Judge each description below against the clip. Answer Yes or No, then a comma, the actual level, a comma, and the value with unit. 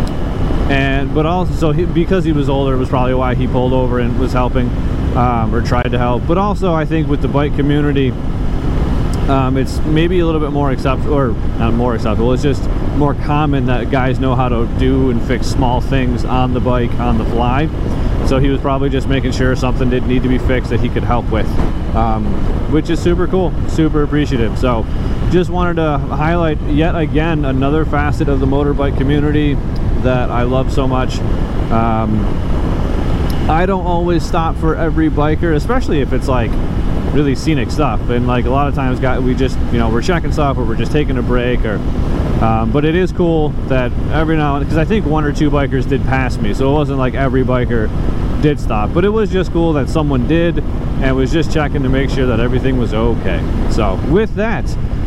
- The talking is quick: Yes, fast, 210 wpm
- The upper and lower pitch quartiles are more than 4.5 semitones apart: No, average, 3.6 semitones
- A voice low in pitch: Yes, low, 130 Hz